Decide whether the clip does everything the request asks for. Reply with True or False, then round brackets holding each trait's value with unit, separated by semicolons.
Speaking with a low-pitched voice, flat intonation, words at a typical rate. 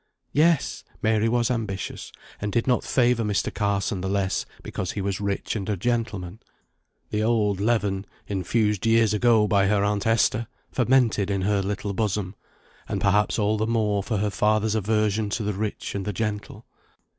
True (105 Hz; 2.1 semitones; 170 wpm)